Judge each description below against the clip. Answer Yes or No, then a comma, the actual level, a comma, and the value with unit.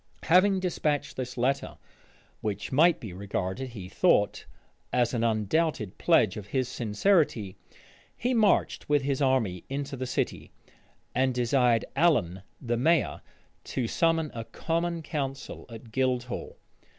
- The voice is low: Yes, low, 130 Hz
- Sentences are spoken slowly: Yes, slow, 130 wpm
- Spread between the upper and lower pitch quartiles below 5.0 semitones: No, wide, 5.6 semitones